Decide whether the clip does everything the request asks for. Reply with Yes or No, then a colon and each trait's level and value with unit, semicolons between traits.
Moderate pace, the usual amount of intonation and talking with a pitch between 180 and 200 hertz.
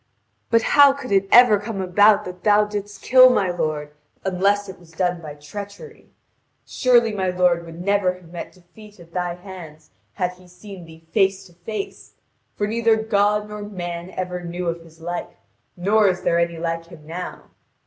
Yes: average, 180 wpm; average, 3.3 semitones; medium, 185 Hz